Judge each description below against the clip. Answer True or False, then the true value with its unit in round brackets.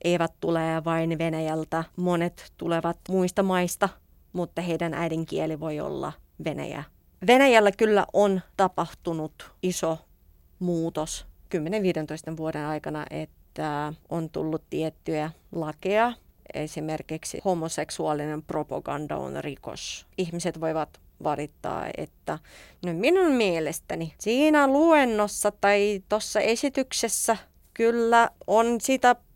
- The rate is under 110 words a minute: True (100 wpm)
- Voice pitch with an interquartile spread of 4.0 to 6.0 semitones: True (4.7 semitones)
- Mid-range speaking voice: True (170 Hz)